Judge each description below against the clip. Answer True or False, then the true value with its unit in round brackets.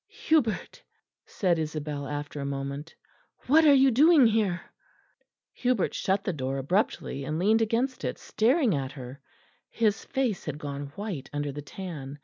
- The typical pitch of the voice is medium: True (175 Hz)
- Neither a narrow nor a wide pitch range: False (8.2 semitones)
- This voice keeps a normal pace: True (150 wpm)